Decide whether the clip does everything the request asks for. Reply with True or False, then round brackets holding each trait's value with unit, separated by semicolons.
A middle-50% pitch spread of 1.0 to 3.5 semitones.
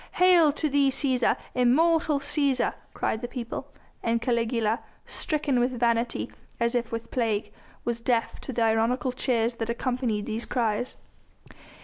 True (2.5 semitones)